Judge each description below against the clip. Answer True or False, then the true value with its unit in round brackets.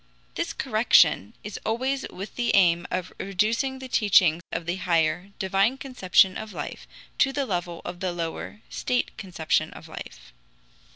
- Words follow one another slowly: False (155 wpm)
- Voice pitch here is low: False (190 Hz)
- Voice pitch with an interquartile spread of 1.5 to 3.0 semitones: False (5.0 semitones)